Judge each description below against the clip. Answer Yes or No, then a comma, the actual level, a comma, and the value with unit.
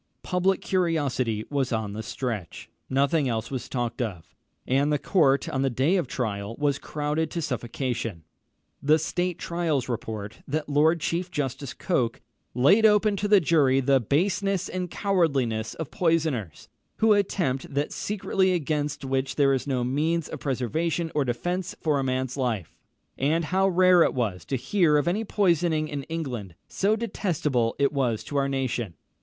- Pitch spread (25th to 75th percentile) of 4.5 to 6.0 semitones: Yes, average, 5.2 semitones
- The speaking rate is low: No, average, 165 wpm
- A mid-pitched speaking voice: Yes, medium, 145 Hz